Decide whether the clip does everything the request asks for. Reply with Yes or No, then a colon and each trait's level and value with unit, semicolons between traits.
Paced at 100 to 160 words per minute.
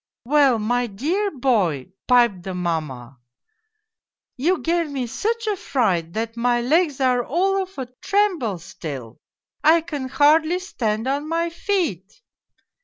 Yes: average, 150 wpm